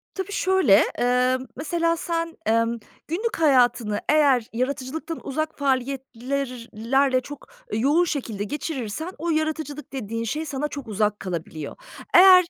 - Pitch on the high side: Yes, very high, 275 Hz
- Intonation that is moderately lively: Yes, average, 4.8 semitones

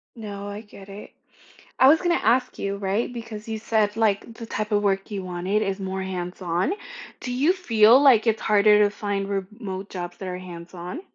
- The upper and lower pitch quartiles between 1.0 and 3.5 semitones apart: Yes, average, 2.7 semitones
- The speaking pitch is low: No, high, 205 Hz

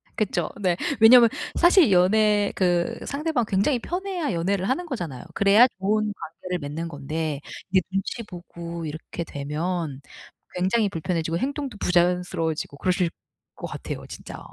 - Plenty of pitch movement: No, average, 4.9 semitones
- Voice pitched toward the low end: No, medium, 185 Hz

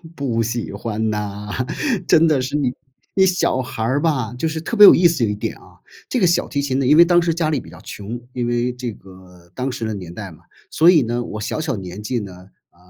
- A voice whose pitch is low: Yes, low, 120 Hz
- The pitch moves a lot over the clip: Yes, wide, 6.7 semitones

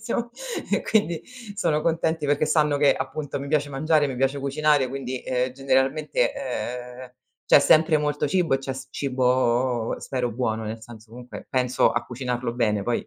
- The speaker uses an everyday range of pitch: Yes, average, 3.3 semitones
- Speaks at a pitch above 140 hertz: No, low, 135 Hz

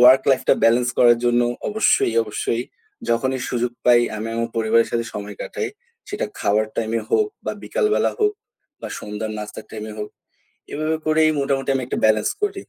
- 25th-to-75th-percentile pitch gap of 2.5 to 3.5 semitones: No, average, 4.1 semitones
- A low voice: Yes, low, 120 Hz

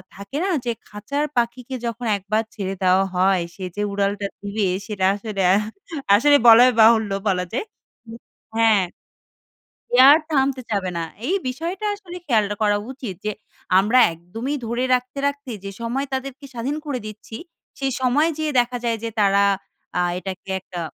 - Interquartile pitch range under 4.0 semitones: No, average, 4.8 semitones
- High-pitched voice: Yes, high, 230 Hz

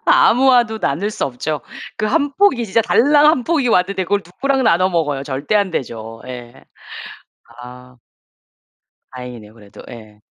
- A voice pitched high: No, medium, 180 Hz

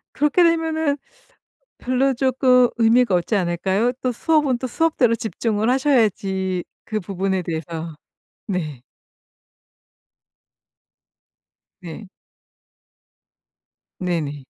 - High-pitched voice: Yes, high, 220 Hz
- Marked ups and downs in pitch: Yes, wide, 6.1 semitones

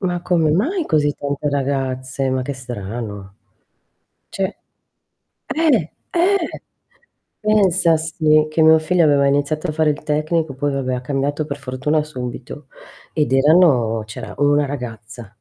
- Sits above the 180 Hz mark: No, medium, 145 Hz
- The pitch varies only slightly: No, average, 3.5 semitones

